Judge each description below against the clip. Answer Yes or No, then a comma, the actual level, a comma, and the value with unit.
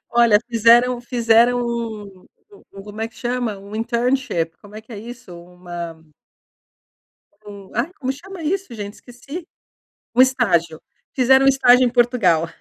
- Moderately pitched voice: No, high, 235 Hz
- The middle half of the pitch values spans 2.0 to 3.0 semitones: No, average, 3.8 semitones